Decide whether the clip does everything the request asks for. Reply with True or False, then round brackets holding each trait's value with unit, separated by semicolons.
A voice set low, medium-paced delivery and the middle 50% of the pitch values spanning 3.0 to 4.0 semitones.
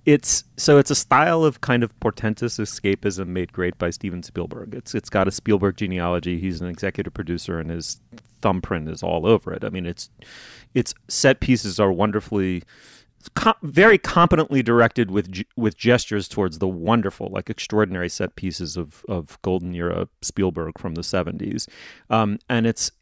False (100 Hz; 170 wpm; 4.8 semitones)